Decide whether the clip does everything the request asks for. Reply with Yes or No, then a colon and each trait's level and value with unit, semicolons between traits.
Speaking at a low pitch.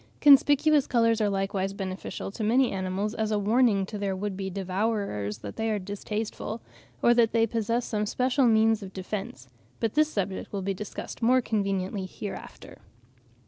No: high, 210 Hz